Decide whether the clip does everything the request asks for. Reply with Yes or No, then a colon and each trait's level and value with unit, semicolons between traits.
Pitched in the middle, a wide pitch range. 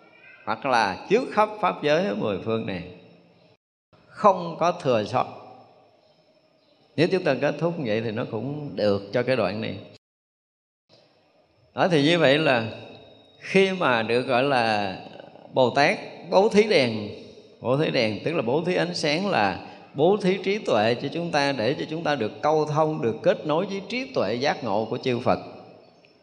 Yes: medium, 145 Hz; wide, 6.0 semitones